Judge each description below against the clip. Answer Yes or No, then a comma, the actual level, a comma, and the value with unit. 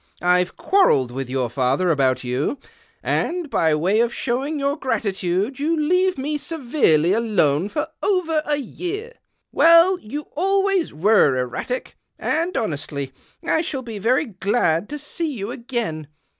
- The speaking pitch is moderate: No, high, 235 Hz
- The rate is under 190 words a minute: Yes, average, 145 wpm